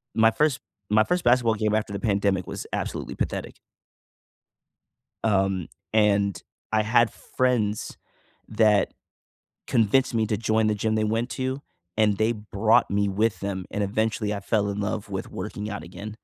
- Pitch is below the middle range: Yes, low, 110 Hz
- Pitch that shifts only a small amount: Yes, narrow, 1.9 semitones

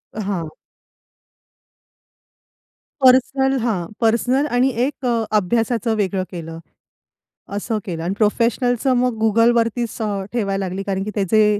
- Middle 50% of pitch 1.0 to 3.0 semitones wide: No, average, 3.8 semitones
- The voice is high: Yes, high, 225 Hz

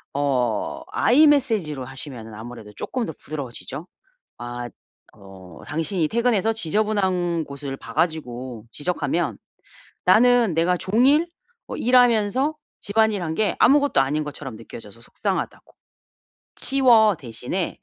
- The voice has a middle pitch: Yes, medium, 165 Hz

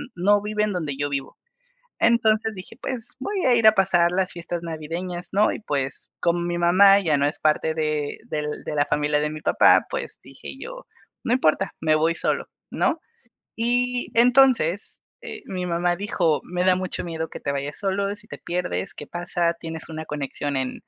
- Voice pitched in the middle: Yes, medium, 175 Hz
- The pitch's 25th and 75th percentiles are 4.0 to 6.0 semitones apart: Yes, average, 5.1 semitones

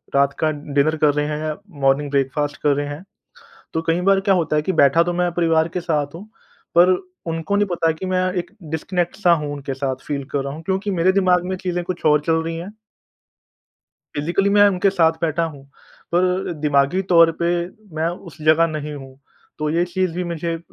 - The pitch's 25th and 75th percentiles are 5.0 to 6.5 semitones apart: No, average, 3.2 semitones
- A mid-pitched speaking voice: Yes, medium, 165 Hz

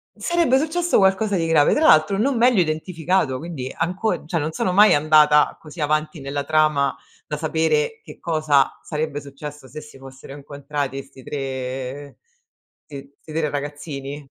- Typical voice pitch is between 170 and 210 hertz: No, medium, 150 Hz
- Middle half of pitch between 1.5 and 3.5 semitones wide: Yes, average, 2.9 semitones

